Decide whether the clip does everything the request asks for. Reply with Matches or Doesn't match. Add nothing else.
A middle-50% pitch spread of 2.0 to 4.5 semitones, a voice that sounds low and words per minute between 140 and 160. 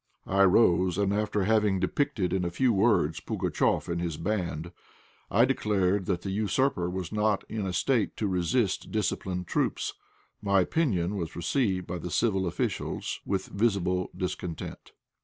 Matches